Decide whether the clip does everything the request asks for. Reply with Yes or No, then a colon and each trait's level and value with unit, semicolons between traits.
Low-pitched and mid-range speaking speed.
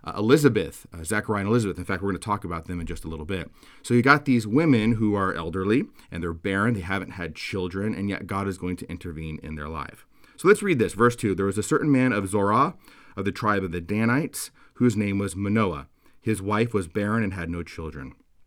No: low, 100 Hz; fast, 245 wpm